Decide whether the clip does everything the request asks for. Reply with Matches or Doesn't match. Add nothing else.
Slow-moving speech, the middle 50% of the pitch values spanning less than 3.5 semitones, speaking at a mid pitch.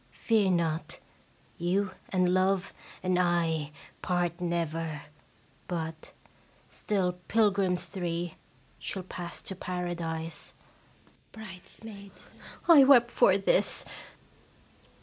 Matches